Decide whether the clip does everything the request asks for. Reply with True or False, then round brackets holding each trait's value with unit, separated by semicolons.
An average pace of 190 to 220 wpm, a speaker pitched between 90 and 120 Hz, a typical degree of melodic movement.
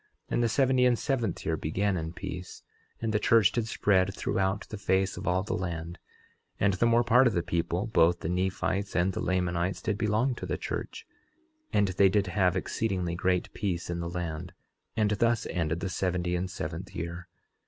True (195 wpm; 95 Hz; 3.3 semitones)